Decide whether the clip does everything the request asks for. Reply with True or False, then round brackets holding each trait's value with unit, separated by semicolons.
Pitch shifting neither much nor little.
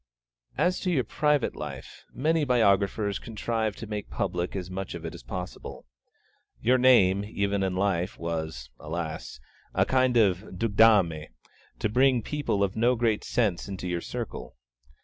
True (4.8 semitones)